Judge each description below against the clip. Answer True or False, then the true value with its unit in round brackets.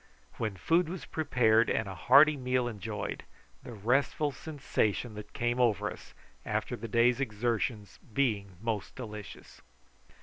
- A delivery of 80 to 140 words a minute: True (135 wpm)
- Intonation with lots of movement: False (3.5 semitones)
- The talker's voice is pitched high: False (120 Hz)